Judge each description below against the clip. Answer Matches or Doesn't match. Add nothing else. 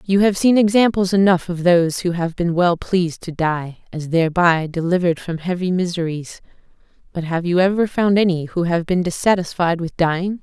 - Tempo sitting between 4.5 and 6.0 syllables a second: Matches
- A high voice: Doesn't match